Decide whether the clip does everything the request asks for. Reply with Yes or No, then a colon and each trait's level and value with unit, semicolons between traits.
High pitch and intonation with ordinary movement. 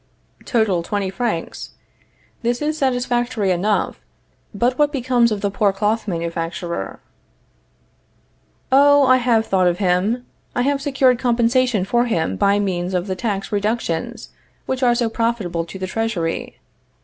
Yes: high, 220 Hz; average, 4.8 semitones